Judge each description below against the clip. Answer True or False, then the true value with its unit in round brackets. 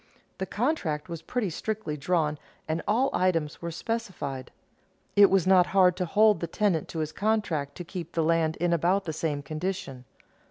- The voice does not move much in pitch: False (4.1 semitones)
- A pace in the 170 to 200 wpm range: True (175 wpm)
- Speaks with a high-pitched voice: False (175 Hz)